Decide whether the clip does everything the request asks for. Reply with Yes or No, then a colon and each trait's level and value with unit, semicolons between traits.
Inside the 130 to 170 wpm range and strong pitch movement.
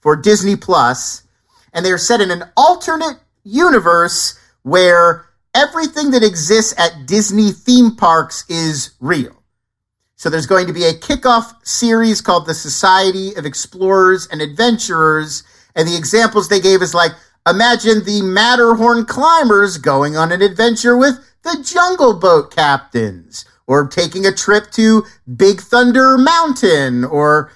Yes: average, 140 wpm; wide, 6.3 semitones